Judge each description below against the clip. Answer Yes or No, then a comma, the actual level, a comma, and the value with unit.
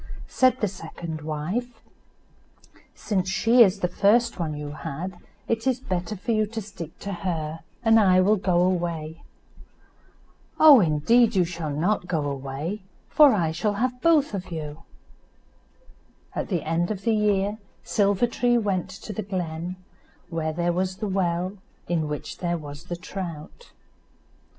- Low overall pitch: No, medium, 185 Hz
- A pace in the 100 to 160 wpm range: Yes, average, 155 wpm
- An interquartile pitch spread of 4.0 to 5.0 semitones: Yes, average, 4.5 semitones